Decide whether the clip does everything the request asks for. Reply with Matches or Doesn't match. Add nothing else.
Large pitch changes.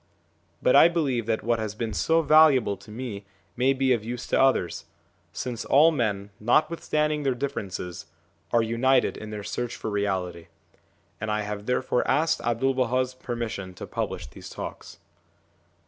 Doesn't match